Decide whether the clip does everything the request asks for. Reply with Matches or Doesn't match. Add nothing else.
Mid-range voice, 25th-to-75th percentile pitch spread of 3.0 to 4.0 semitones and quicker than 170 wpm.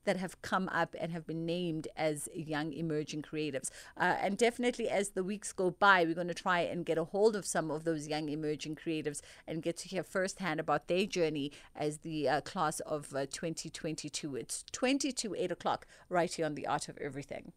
Matches